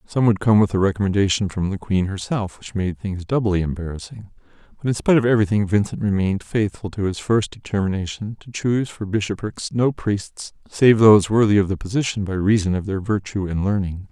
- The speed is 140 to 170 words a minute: No, average, 195 wpm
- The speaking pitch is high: No, low, 100 Hz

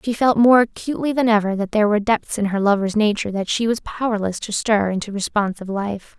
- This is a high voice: Yes, high, 210 Hz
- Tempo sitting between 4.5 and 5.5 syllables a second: No, 6.2 syllables/s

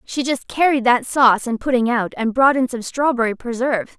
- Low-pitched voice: No, very high, 250 Hz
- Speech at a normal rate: No, fast, 210 wpm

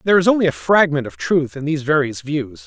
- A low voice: No, medium, 145 Hz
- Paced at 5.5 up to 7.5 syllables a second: Yes, 6.3 syllables/s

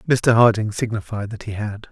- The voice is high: No, low, 110 Hz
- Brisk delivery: No, average, 190 wpm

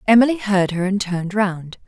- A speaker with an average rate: Yes, average, 190 wpm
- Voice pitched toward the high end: Yes, high, 200 Hz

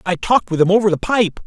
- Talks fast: Yes, fast, 285 wpm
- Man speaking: Yes, male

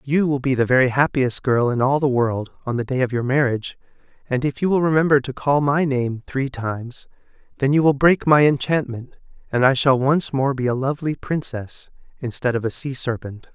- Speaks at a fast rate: Yes, fast, 215 wpm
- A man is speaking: Yes, male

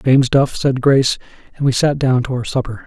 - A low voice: Yes, low, 130 Hz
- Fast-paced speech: Yes, fast, 230 wpm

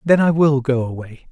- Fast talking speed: Yes, fast, 230 wpm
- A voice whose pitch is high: No, medium, 140 Hz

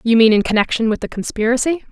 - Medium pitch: No, high, 235 Hz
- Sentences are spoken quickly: Yes, fast, 220 wpm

